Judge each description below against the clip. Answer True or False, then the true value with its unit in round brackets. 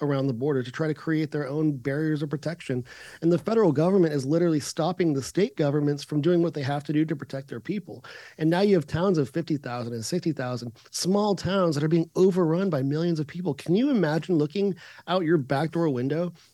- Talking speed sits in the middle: False (220 wpm)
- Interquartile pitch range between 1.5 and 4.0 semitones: True (3.2 semitones)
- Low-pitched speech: False (155 Hz)